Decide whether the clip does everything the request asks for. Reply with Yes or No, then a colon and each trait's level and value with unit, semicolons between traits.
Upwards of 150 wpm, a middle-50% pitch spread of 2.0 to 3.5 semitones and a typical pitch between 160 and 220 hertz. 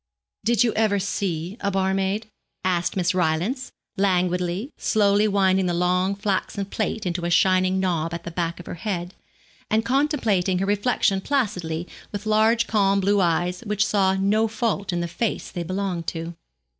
Yes: average, 165 wpm; average, 2.9 semitones; high, 190 Hz